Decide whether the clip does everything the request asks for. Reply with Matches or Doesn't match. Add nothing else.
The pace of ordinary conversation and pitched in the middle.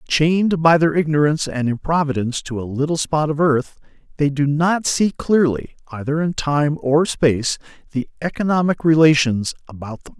Matches